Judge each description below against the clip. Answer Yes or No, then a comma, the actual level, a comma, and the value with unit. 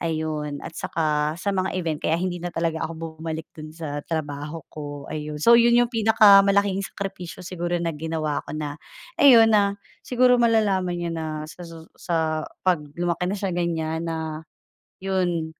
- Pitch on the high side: No, medium, 165 Hz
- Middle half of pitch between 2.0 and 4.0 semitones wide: Yes, average, 3.5 semitones